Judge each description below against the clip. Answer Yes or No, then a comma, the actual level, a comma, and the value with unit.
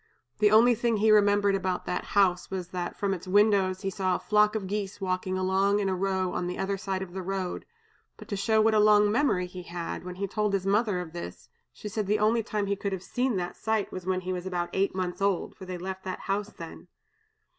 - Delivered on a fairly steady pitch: Yes, narrow, 2.1 semitones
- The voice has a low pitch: No, high, 195 Hz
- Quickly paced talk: Yes, fast, 245 wpm